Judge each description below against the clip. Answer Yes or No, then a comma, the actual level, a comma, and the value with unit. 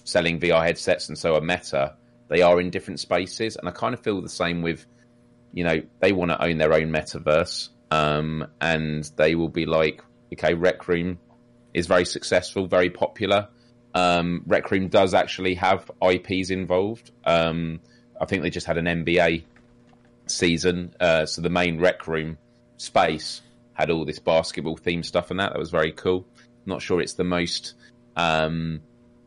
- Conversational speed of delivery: Yes, average, 175 wpm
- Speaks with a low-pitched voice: Yes, very low, 85 Hz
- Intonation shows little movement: No, average, 3.1 semitones